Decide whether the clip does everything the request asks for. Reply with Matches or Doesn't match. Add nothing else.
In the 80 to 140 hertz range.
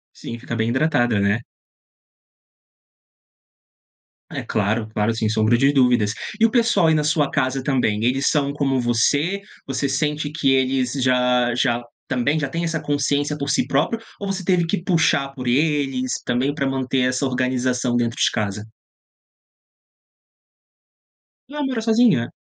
Matches